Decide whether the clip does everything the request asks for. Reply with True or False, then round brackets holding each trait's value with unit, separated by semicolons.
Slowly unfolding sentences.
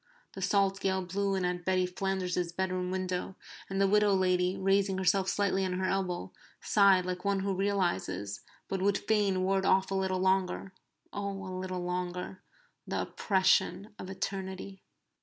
False (160 wpm)